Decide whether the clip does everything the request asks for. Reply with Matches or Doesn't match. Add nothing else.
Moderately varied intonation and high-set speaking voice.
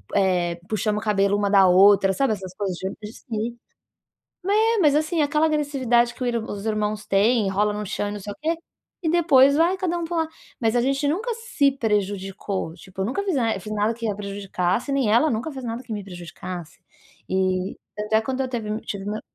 Doesn't match